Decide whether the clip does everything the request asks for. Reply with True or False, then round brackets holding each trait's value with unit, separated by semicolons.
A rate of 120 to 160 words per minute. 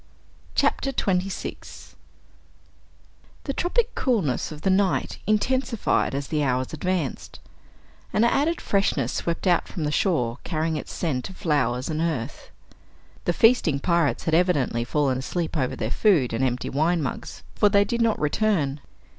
True (145 wpm)